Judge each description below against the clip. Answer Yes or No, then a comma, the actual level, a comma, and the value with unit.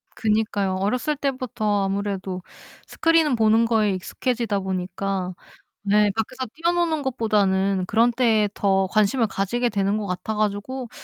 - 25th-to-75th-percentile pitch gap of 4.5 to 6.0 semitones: No, average, 3.6 semitones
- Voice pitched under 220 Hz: Yes, high, 210 Hz